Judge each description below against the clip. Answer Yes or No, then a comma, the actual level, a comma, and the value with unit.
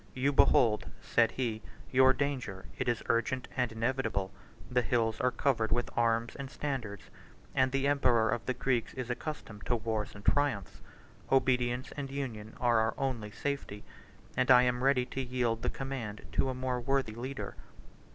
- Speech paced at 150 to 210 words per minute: Yes, average, 170 wpm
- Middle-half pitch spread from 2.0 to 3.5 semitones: Yes, average, 2.8 semitones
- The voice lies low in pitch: Yes, low, 125 Hz